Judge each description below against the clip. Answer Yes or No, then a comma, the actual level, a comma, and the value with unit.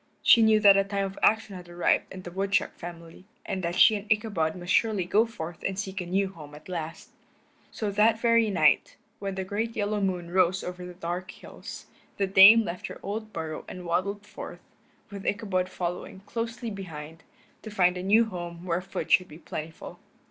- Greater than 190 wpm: Yes, average, 200 wpm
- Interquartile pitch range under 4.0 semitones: Yes, average, 2.9 semitones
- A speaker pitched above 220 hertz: No, high, 190 Hz